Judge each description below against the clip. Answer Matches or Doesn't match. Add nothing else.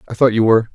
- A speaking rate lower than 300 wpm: Doesn't match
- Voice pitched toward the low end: Matches